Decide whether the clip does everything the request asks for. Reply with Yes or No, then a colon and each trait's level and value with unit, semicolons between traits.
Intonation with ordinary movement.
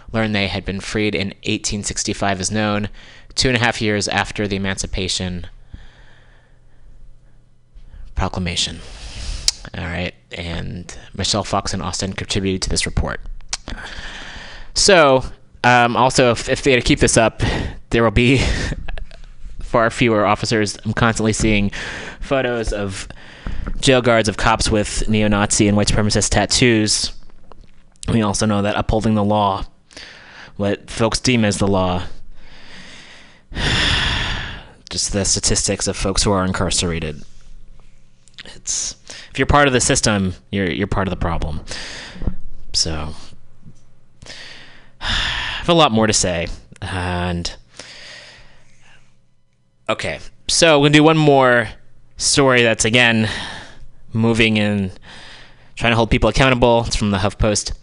Yes: average, 4.0 semitones